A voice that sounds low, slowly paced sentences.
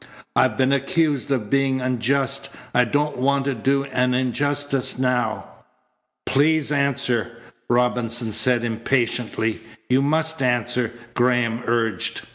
Yes: low, 125 Hz; slow, 115 wpm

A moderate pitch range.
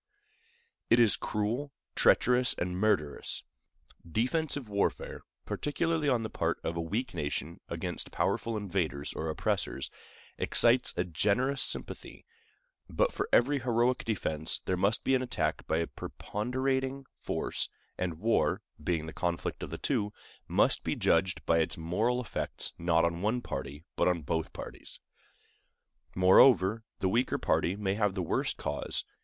No: wide, 6.8 semitones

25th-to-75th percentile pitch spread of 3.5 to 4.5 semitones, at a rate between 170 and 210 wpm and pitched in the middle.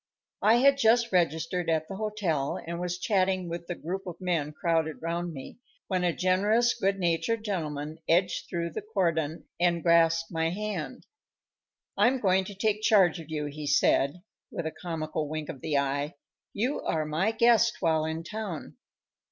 Yes: average, 4.0 semitones; average, 175 wpm; medium, 175 Hz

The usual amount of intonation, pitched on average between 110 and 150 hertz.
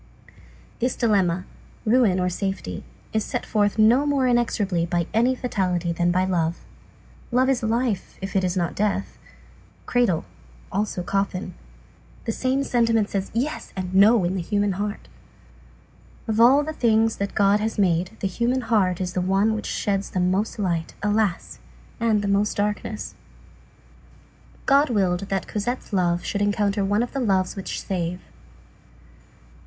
No: average, 3.6 semitones; high, 205 Hz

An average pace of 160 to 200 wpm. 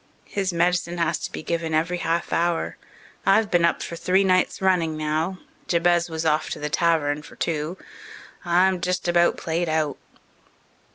Yes: average, 165 wpm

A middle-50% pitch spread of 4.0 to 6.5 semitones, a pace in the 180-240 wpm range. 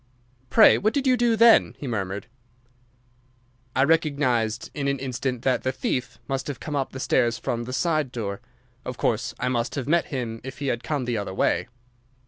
No: average, 3.5 semitones; average, 195 wpm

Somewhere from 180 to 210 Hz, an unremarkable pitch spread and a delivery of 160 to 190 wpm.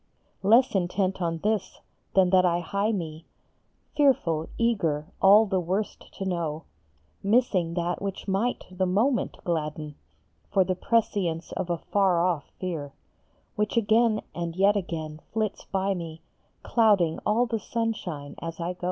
No: medium, 185 Hz; average, 3.9 semitones; average, 145 wpm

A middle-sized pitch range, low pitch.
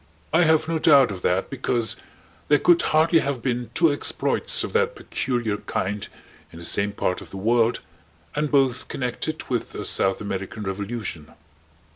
No: wide, 6.7 semitones; low, 120 Hz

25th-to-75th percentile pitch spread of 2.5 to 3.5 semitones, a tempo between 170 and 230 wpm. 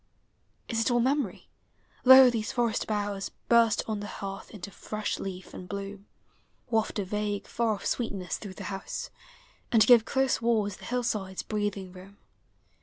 No: average, 2.8 semitones; average, 160 wpm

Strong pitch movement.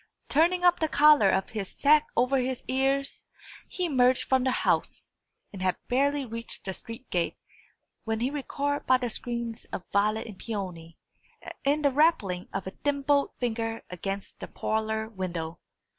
Yes: wide, 5.7 semitones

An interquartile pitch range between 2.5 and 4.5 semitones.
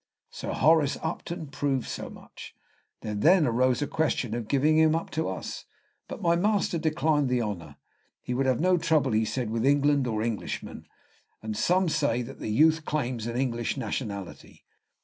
No: average, 5.3 semitones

